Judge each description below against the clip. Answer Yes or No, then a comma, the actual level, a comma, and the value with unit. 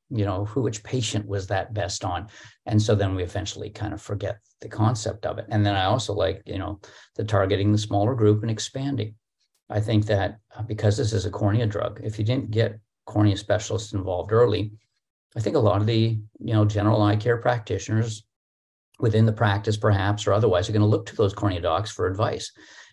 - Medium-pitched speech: No, low, 105 Hz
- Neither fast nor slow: No, fast, 210 wpm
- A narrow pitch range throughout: Yes, narrow, 1.5 semitones